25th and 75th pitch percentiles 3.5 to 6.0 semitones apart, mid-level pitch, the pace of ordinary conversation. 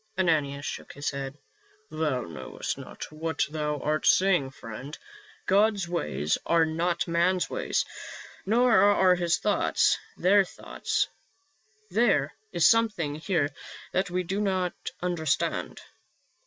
No: average, 4.5 semitones; medium, 170 Hz; slow, 125 wpm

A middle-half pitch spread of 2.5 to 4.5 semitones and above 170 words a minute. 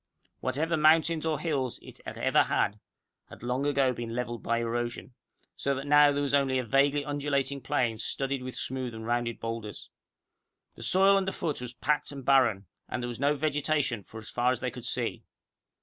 Yes: average, 3.3 semitones; average, 190 wpm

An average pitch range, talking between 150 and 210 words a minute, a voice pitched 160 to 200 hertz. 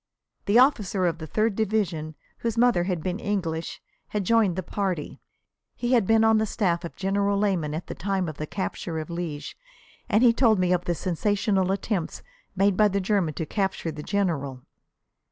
Yes: average, 3.7 semitones; average, 190 wpm; high, 190 Hz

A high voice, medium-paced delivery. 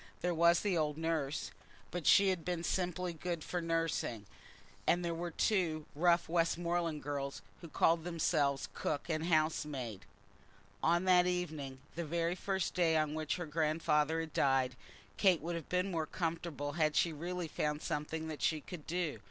No: medium, 165 Hz; average, 170 wpm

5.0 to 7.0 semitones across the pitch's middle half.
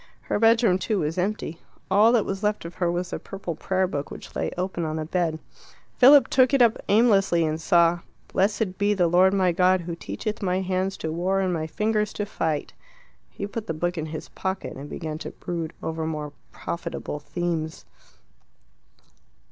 No: average, 3.7 semitones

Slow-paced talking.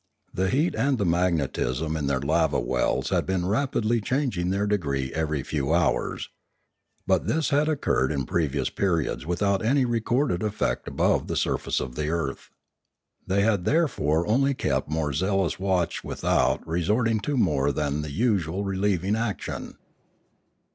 No: average, 150 wpm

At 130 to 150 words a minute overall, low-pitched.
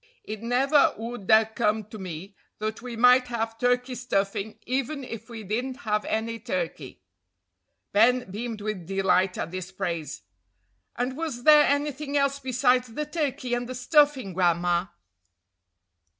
No: average, 145 wpm; high, 230 Hz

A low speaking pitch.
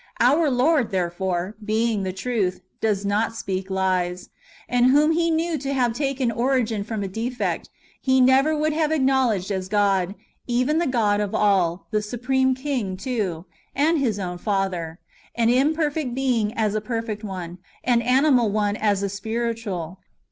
No: high, 225 Hz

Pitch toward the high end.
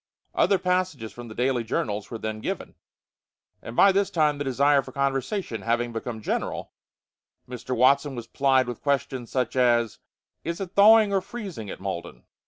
No: low, 130 Hz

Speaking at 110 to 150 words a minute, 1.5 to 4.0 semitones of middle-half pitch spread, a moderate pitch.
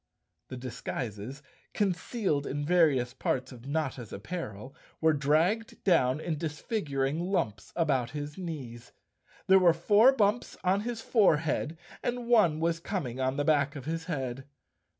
No: average, 140 wpm; wide, 5.5 semitones; medium, 155 Hz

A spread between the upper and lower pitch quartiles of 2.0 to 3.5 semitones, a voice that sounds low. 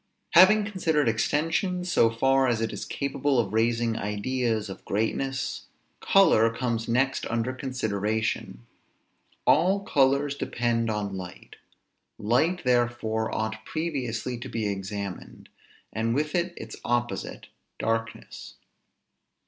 No: average, 4.0 semitones; low, 120 Hz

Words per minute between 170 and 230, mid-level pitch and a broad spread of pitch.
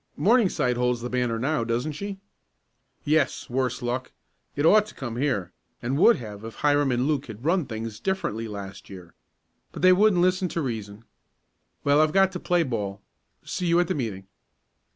No: average, 180 wpm; low, 130 Hz; wide, 6.9 semitones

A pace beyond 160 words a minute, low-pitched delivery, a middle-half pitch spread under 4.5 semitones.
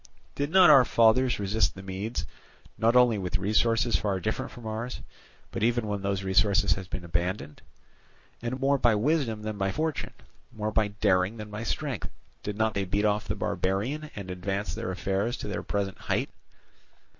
Yes: average, 180 wpm; low, 105 Hz; average, 3.3 semitones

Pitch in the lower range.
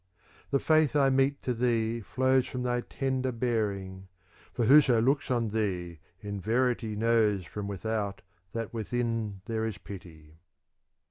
Yes: low, 115 Hz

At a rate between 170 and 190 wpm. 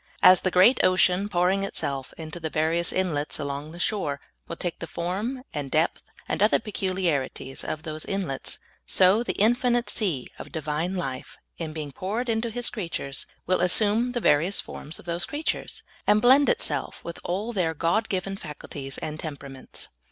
Yes: average, 175 wpm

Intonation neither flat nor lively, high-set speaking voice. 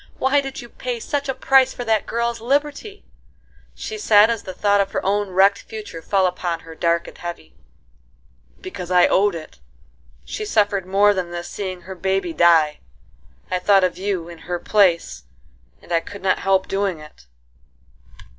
Yes: average, 4.2 semitones; high, 195 Hz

